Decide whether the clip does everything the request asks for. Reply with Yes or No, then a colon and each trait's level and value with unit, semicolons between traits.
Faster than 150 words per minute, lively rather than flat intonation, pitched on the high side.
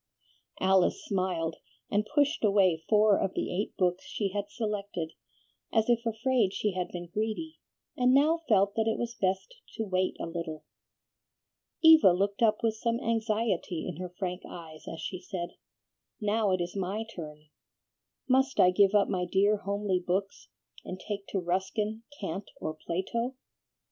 No: average, 160 wpm; average, 3.5 semitones; high, 200 Hz